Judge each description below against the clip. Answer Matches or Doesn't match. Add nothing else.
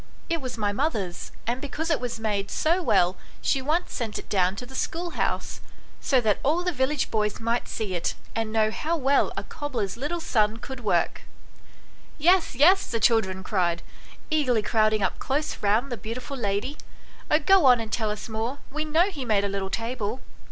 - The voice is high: Matches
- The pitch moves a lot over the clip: Matches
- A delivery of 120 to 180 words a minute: Doesn't match